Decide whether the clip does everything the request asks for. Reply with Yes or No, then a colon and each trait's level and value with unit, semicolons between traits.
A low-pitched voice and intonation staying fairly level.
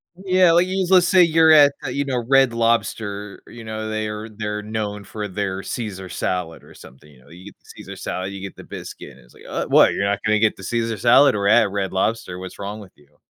No: low, 105 Hz; average, 3.4 semitones